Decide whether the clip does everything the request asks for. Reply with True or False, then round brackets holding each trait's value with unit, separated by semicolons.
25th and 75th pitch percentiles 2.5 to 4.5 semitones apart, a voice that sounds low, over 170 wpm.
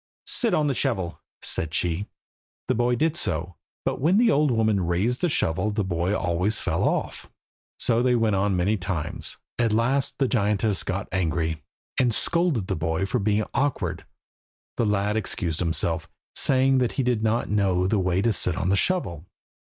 False (5.3 semitones; 105 Hz; 185 wpm)